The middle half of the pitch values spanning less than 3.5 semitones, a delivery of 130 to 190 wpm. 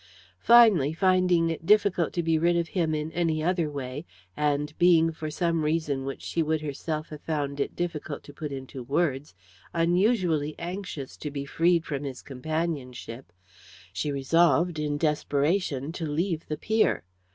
Yes: average, 3.0 semitones; average, 160 wpm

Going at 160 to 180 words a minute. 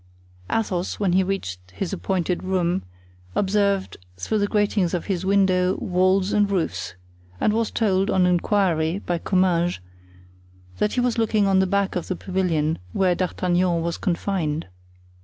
No: average, 150 wpm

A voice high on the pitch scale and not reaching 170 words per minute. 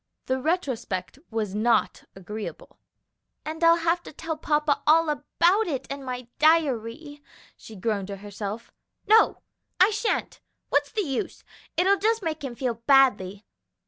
Yes: very high, 280 Hz; average, 145 wpm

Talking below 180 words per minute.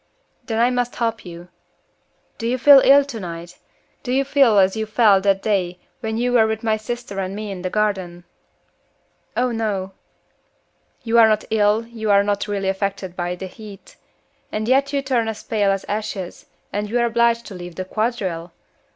No: average, 185 wpm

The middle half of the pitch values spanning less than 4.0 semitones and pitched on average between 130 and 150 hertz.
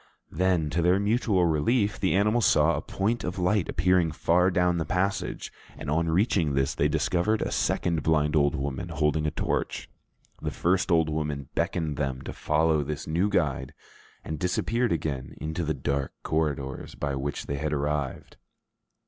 No: average, 3.6 semitones; very low, 80 Hz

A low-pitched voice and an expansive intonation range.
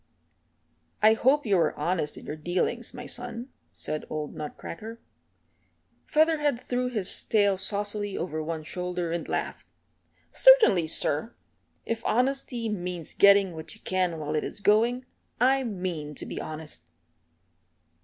No: high, 200 Hz; wide, 6.3 semitones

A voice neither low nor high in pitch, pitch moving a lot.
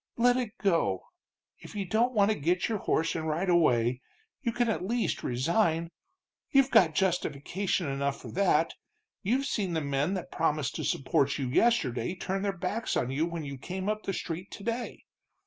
Yes: medium, 180 Hz; wide, 5.9 semitones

